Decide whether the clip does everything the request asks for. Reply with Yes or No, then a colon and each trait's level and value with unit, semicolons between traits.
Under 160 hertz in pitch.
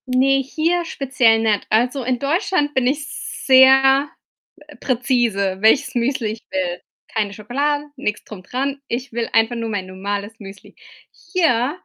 No: very high, 250 Hz